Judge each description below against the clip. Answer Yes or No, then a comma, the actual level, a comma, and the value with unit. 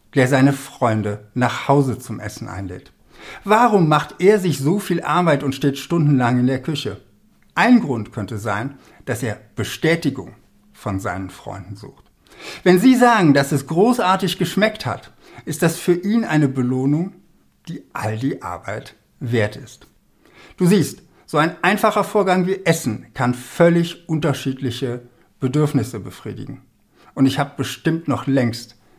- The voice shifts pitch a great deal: Yes, wide, 5.9 semitones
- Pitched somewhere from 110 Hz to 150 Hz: Yes, medium, 140 Hz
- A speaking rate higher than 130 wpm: Yes, average, 145 wpm